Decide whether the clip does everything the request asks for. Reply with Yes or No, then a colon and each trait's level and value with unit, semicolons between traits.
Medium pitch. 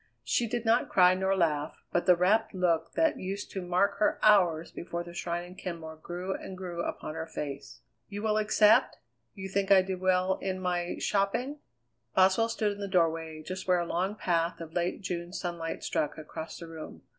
Yes: medium, 180 Hz